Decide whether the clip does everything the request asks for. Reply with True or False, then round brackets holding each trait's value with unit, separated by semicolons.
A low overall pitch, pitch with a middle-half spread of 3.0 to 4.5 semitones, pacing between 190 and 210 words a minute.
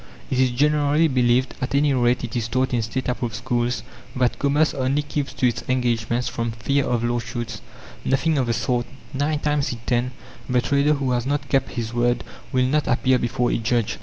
False (125 Hz; 2.6 semitones; 200 wpm)